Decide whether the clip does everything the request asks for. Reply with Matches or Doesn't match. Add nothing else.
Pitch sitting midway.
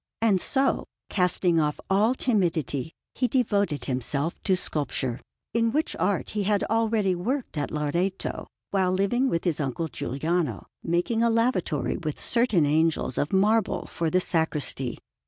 Matches